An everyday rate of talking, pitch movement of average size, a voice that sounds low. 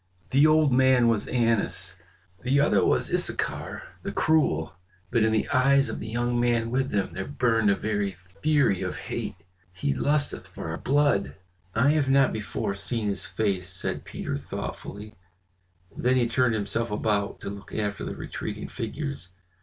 Yes: average, 165 wpm; average, 4.6 semitones; low, 115 Hz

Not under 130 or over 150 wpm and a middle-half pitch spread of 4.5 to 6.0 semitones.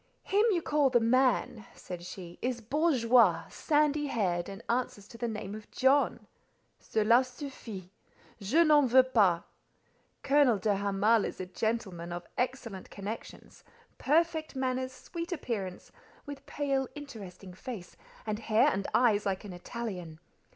Yes: slow, 135 wpm; wide, 5.4 semitones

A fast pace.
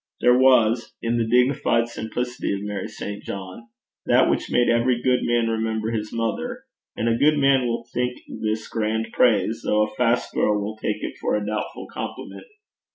No: average, 180 wpm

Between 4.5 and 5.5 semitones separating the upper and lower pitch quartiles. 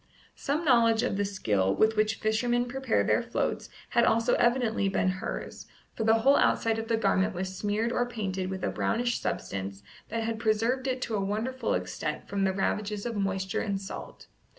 No: average, 3.5 semitones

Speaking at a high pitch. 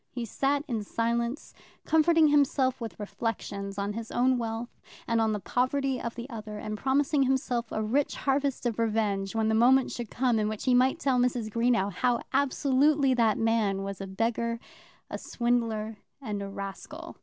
Yes: high, 235 Hz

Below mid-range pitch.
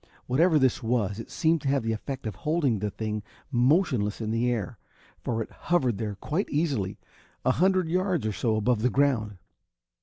Yes: low, 125 Hz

